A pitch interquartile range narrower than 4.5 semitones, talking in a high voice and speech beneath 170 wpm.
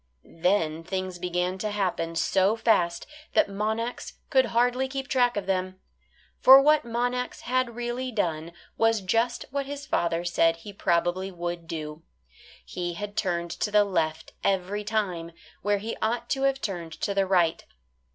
No: wide, 5.5 semitones; high, 200 Hz; average, 160 wpm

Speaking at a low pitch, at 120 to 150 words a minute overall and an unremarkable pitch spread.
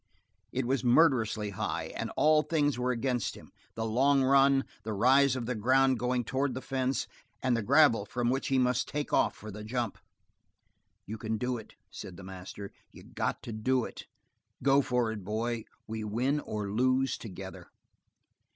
No: low, 125 Hz; average, 180 wpm; average, 3.5 semitones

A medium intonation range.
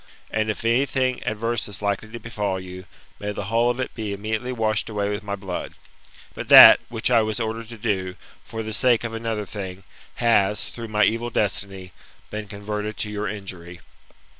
No: narrow, 2.2 semitones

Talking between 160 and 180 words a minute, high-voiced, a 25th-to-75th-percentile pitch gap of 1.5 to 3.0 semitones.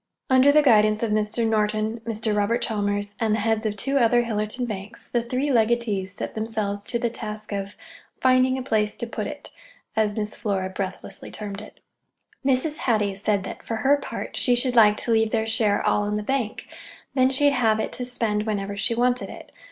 No: average, 200 wpm; high, 220 Hz; narrow, 2.6 semitones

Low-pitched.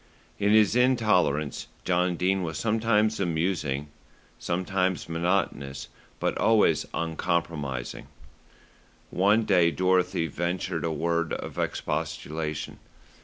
Yes: very low, 85 Hz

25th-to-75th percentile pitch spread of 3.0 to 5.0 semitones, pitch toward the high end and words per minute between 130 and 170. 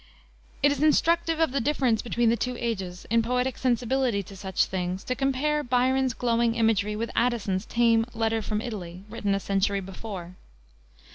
Yes: average, 4.0 semitones; high, 230 Hz; average, 165 wpm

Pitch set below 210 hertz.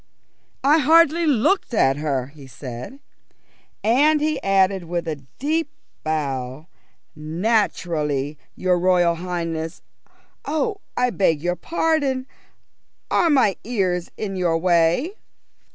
Yes: medium, 185 Hz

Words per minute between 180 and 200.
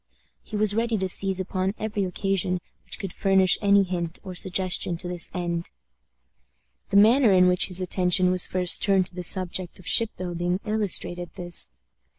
No: average, 170 wpm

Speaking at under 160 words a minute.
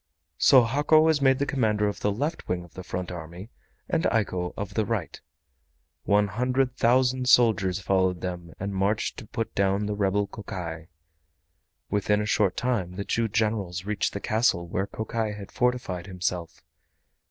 No: average, 165 wpm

